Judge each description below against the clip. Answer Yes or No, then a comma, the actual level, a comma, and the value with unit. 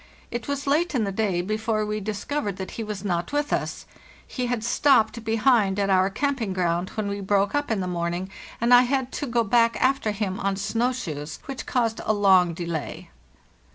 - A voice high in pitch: Yes, high, 215 Hz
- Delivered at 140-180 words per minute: No, fast, 205 wpm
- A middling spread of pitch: Yes, average, 4.2 semitones